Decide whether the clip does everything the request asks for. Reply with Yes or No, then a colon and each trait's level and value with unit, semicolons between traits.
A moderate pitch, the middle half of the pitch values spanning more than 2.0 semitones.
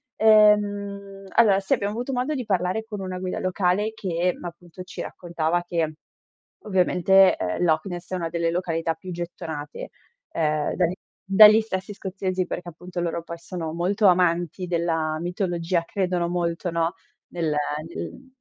Yes: medium, 180 Hz; narrow, 2.6 semitones